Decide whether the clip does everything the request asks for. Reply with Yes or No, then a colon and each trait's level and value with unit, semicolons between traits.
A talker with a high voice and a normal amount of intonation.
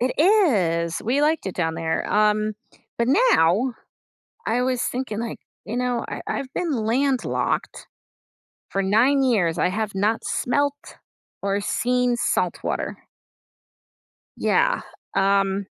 Yes: high, 235 Hz; average, 4.9 semitones